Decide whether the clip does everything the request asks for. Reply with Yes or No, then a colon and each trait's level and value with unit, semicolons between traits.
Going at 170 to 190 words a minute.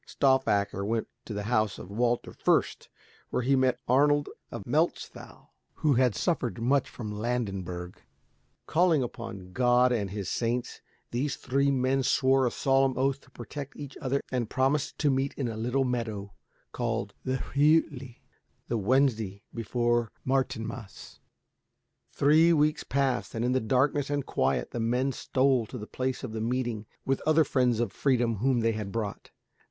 No: average, 160 wpm